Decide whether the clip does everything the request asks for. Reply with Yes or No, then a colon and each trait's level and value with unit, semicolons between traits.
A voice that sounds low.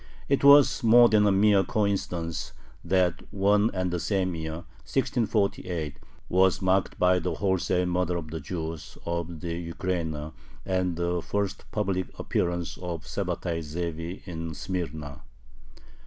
Yes: very low, 90 Hz